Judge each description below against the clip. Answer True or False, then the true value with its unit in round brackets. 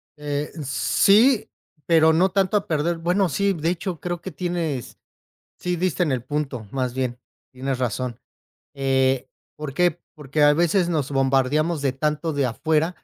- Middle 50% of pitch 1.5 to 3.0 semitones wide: False (4.5 semitones)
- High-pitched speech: False (150 Hz)